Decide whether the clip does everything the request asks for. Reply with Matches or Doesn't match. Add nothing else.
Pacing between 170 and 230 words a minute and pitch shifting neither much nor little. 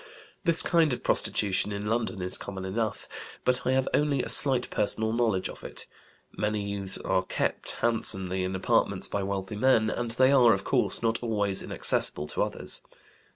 Matches